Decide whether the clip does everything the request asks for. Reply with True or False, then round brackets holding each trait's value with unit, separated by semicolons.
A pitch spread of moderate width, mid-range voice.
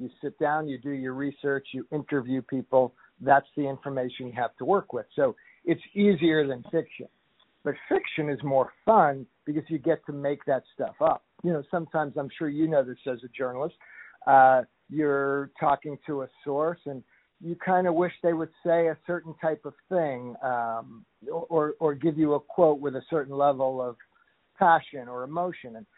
True (3.5 semitones; 145 Hz)